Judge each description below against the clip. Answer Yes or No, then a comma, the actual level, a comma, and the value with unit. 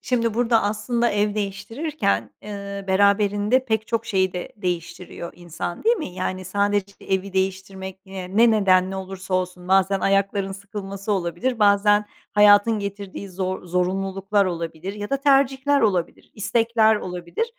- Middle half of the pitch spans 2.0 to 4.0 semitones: Yes, narrow, 2.4 semitones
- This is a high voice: Yes, high, 200 Hz